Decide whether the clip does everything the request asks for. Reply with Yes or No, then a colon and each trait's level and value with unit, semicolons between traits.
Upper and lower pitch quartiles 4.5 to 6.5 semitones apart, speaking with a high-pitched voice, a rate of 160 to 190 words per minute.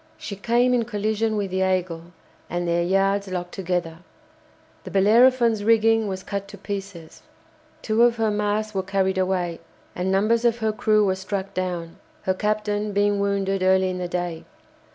No: narrow, 2.5 semitones; high, 200 Hz; average, 170 wpm